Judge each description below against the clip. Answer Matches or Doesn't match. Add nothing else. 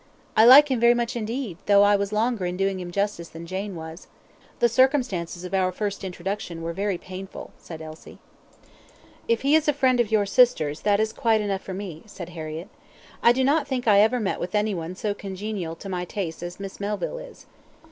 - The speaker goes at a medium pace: Doesn't match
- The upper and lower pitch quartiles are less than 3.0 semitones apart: Doesn't match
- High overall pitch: Matches